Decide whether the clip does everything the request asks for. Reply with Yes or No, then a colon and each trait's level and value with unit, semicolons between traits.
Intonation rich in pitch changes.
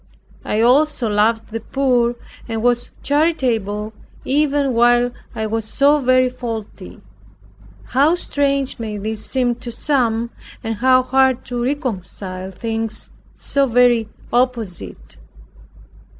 No: average, 2.9 semitones